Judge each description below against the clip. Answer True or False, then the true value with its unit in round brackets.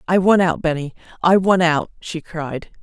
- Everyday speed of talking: True (170 wpm)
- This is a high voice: False (170 Hz)